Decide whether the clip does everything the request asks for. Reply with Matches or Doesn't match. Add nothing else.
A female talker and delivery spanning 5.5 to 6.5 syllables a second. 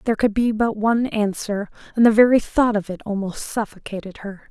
Matches